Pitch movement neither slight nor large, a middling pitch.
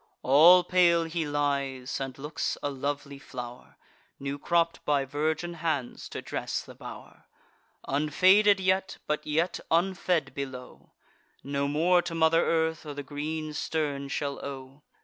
Yes: average, 3.1 semitones; medium, 150 Hz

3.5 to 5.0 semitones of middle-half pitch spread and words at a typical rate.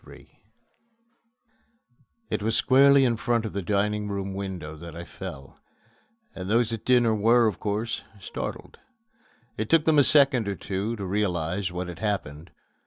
Yes: average, 4.0 semitones; average, 160 wpm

